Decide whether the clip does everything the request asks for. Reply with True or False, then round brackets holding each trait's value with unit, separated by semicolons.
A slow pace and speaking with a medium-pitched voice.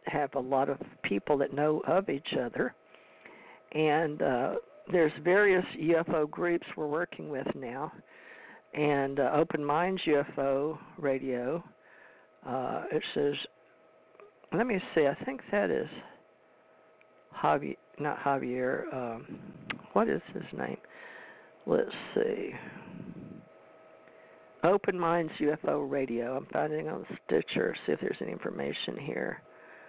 True (120 wpm; 150 Hz)